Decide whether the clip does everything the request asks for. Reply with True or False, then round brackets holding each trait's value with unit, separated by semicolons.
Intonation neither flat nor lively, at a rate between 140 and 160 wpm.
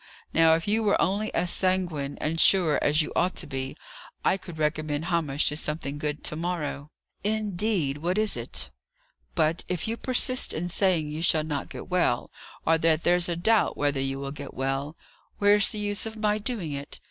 False (4.7 semitones; 195 wpm)